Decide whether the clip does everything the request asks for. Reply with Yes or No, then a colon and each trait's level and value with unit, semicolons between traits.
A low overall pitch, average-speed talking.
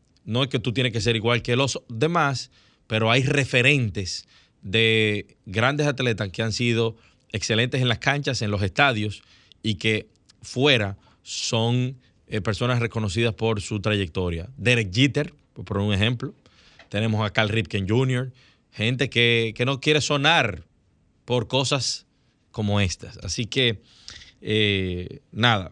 Yes: low, 115 Hz; average, 140 wpm